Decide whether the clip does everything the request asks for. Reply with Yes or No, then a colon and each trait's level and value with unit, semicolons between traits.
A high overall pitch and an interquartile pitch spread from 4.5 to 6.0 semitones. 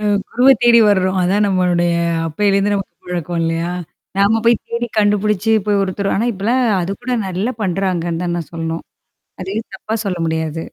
No: high, 195 Hz; average, 3.3 semitones